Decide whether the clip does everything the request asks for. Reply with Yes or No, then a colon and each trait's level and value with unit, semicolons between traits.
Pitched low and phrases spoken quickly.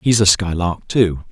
No: very low, 95 Hz; average, 185 wpm